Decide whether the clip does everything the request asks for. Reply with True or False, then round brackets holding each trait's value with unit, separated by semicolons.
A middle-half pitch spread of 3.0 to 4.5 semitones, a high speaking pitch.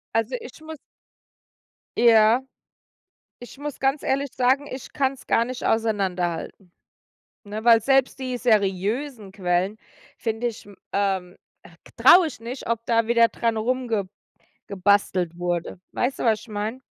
True (4.0 semitones; 225 Hz)